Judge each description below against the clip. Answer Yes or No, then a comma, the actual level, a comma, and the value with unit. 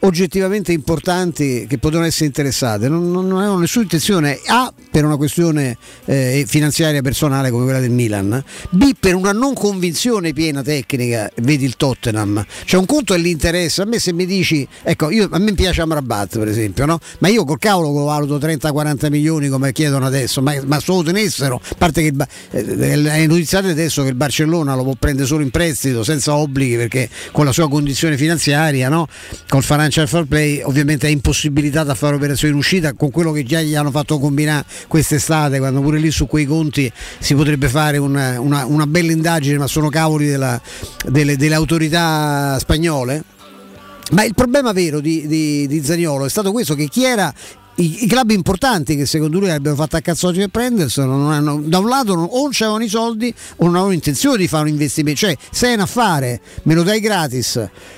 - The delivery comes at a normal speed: No, fast, 195 wpm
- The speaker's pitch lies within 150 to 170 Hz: Yes, medium, 155 Hz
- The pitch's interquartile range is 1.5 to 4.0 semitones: Yes, average, 3.5 semitones